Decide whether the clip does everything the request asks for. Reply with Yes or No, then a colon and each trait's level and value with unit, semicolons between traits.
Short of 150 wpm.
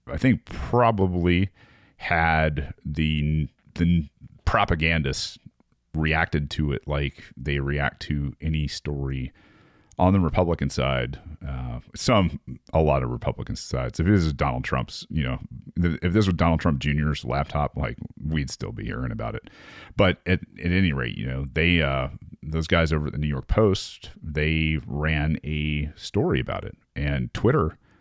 No: average, 160 wpm